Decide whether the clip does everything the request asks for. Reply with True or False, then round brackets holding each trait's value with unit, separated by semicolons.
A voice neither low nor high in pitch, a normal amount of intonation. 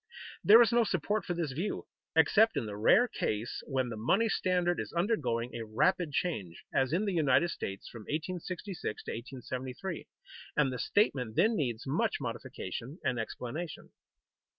False (145 Hz; 7.4 semitones)